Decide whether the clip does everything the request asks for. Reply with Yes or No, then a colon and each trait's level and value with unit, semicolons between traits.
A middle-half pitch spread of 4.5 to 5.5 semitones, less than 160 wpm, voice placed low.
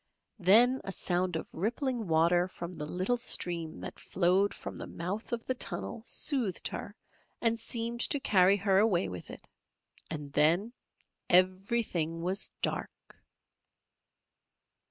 No: average, 5.0 semitones; slow, 135 wpm; medium, 185 Hz